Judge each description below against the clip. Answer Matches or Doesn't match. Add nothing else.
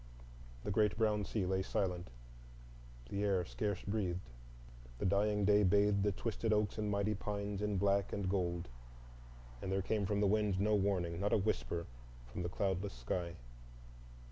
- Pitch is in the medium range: Doesn't match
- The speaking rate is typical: Matches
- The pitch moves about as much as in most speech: Doesn't match